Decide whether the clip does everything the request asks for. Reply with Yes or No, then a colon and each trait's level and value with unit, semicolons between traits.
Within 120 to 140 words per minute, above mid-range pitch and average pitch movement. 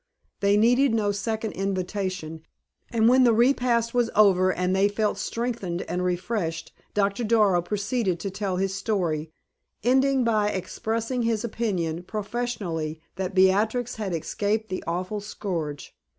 Yes: slow, 135 wpm; high, 205 Hz; average, 3.7 semitones